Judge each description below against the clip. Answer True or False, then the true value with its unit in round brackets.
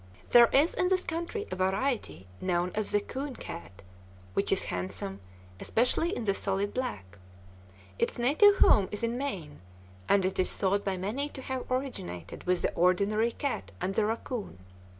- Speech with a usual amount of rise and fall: False (6.3 semitones)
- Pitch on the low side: False (205 Hz)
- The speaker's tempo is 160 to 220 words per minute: True (170 wpm)